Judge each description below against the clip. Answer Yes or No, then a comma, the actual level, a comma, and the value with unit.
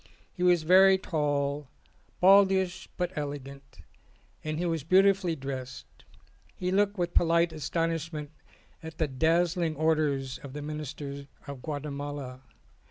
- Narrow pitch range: No, average, 3.8 semitones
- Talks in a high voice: No, medium, 155 Hz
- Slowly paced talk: Yes, slow, 120 wpm